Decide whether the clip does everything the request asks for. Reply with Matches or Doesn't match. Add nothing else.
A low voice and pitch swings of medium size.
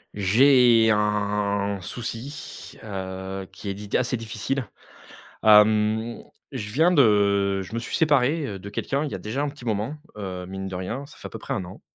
Matches